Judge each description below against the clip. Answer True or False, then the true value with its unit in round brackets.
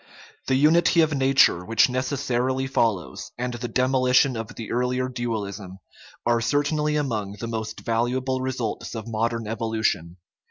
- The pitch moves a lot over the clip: False (2.7 semitones)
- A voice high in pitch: False (120 Hz)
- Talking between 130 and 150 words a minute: True (135 wpm)